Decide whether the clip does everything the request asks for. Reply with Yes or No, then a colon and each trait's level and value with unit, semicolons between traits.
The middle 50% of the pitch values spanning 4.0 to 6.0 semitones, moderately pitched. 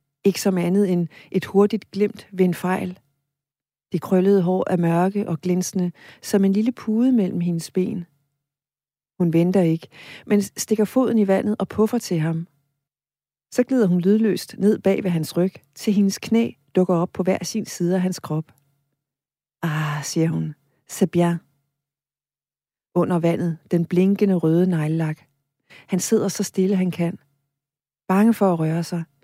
Yes: average, 4.8 semitones; medium, 175 Hz